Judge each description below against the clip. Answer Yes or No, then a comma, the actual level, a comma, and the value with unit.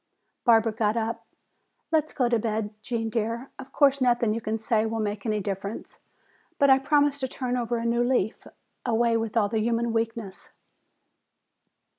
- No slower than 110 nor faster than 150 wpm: No, average, 165 wpm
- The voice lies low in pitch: No, high, 230 Hz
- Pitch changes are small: Yes, narrow, 2.0 semitones